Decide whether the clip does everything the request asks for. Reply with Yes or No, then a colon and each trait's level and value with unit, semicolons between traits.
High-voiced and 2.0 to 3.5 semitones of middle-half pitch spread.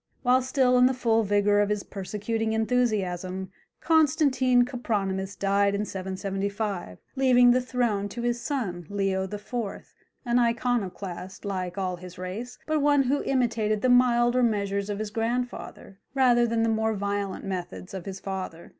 No: high, 215 Hz; average, 4.0 semitones